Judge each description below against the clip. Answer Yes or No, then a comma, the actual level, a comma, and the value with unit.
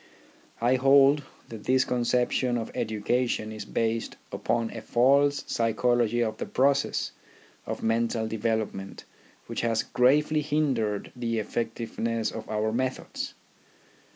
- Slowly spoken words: Yes, slow, 120 wpm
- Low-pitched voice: Yes, low, 120 Hz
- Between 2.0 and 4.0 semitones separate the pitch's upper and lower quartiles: Yes, narrow, 2.6 semitones